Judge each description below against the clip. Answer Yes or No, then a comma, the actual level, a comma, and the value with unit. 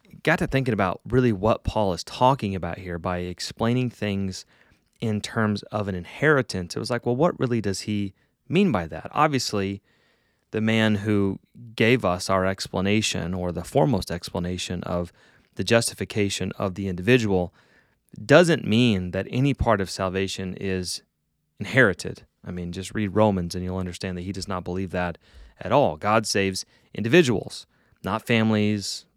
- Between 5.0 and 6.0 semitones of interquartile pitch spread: No, average, 3.9 semitones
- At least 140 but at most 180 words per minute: Yes, average, 160 wpm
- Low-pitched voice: Yes, low, 100 Hz